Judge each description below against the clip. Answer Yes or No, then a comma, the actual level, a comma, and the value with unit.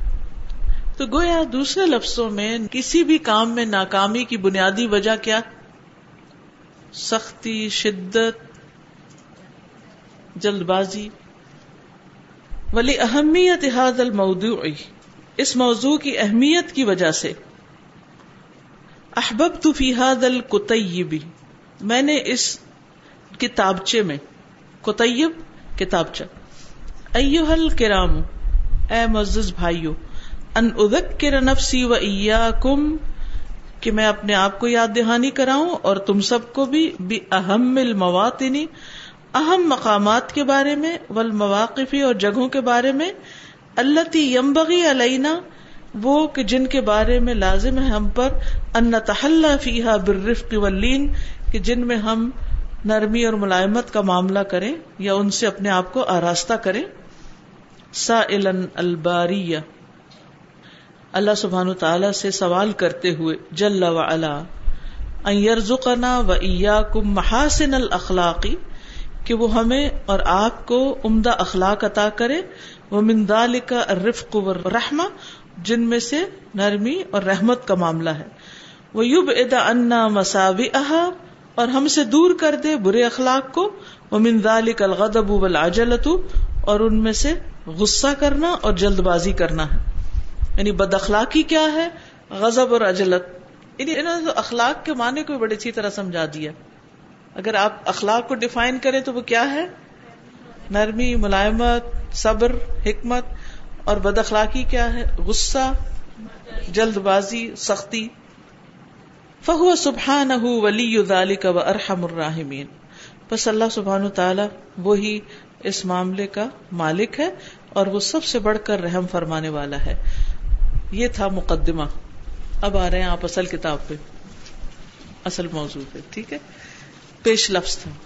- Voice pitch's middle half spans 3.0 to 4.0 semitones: No, average, 4.9 semitones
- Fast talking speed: No, average, 120 wpm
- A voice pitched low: No, high, 220 Hz